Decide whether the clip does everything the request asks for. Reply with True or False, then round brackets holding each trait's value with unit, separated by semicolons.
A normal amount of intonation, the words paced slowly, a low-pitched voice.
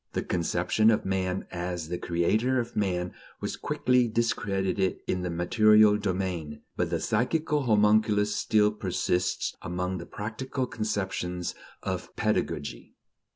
True (3.4 semitones; 125 wpm; 100 Hz)